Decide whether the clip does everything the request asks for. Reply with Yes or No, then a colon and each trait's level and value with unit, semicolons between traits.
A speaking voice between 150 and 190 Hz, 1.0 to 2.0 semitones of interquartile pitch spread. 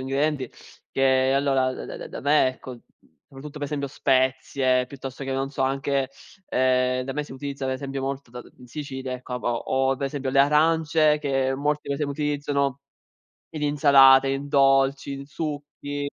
No: low, 135 Hz; narrow, 1.5 semitones